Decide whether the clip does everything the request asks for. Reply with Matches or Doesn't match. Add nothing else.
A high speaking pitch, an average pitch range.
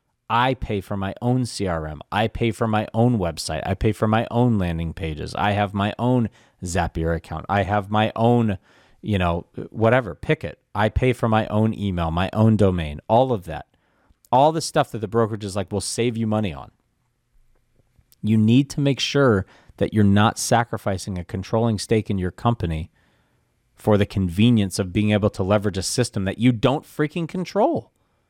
Doesn't match